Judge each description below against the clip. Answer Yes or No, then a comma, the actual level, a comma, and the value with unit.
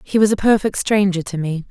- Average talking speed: No, fast, 245 wpm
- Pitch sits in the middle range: No, high, 195 Hz